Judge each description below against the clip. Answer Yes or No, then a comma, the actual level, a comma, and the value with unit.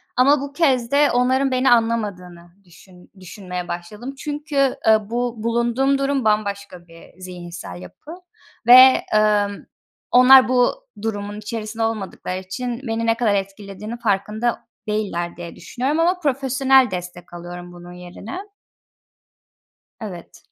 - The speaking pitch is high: Yes, high, 220 Hz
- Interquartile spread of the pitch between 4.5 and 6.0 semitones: Yes, wide, 5.6 semitones